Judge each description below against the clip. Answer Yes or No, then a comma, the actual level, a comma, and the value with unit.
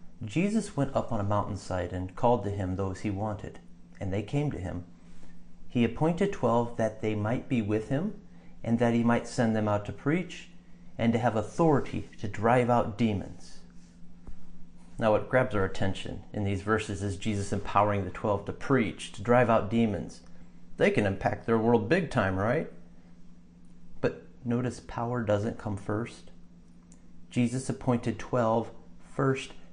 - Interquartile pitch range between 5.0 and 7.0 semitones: Yes, wide, 5.4 semitones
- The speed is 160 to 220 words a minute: Yes, average, 165 wpm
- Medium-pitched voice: No, low, 105 Hz